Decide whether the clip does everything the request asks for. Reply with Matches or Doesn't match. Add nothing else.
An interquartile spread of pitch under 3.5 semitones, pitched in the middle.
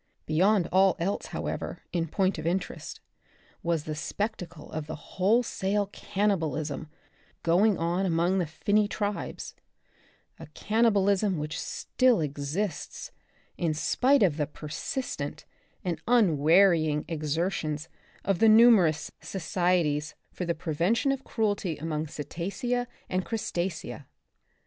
Doesn't match